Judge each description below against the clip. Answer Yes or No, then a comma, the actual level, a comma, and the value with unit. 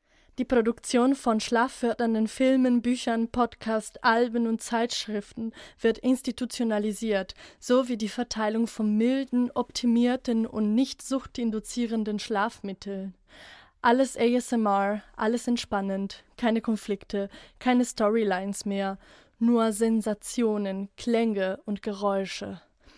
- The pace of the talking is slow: Yes, slow, 95 wpm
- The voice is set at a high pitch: Yes, high, 230 Hz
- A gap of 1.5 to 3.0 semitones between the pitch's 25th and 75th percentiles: Yes, narrow, 2.6 semitones